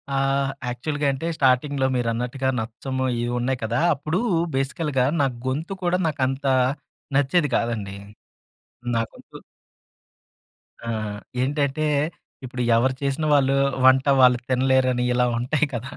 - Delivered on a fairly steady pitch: Yes, narrow, 2.3 semitones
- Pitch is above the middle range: No, low, 130 Hz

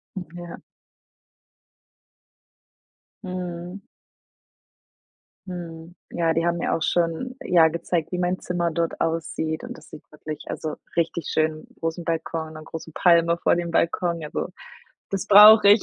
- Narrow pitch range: Yes, narrow, 1.6 semitones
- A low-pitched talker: No, medium, 170 Hz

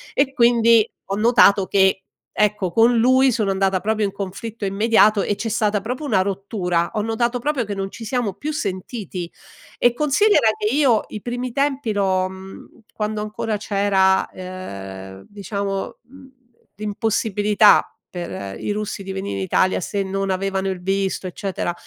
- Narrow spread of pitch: No, average, 3.3 semitones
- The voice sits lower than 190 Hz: No, high, 205 Hz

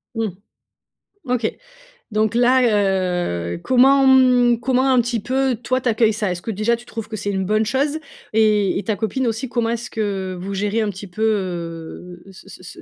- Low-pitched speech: No, high, 220 Hz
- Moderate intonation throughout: Yes, average, 4.1 semitones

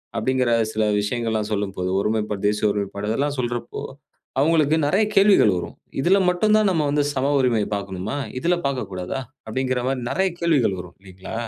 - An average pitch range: No, wide, 5.9 semitones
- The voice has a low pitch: Yes, low, 120 Hz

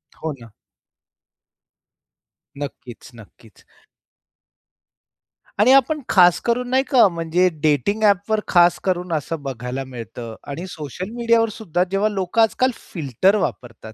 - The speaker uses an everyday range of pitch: No, wide, 7.6 semitones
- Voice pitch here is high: No, medium, 180 Hz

